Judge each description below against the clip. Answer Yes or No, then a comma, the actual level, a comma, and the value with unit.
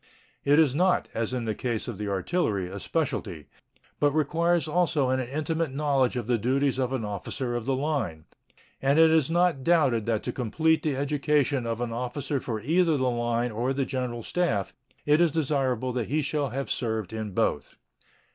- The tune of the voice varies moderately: Yes, average, 4.4 semitones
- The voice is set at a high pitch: No, low, 130 Hz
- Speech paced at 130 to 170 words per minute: No, average, 190 wpm